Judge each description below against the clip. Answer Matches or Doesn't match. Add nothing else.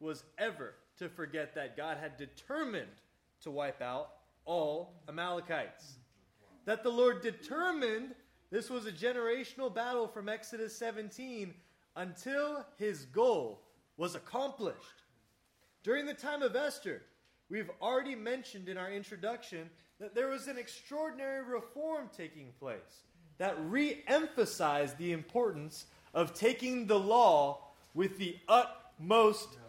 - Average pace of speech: Doesn't match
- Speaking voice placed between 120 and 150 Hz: Doesn't match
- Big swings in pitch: Matches